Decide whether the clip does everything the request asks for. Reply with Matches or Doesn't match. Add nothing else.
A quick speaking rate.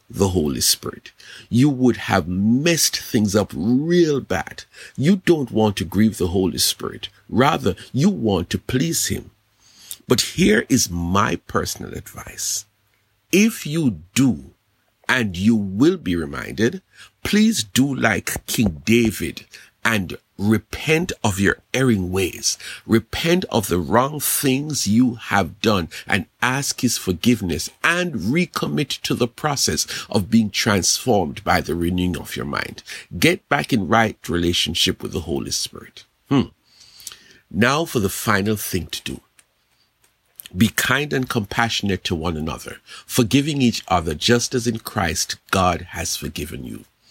Doesn't match